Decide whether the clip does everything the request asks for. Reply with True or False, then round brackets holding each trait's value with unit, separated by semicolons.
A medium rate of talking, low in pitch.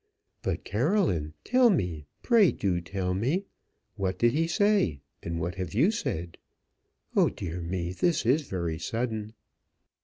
True (145 wpm; 100 Hz)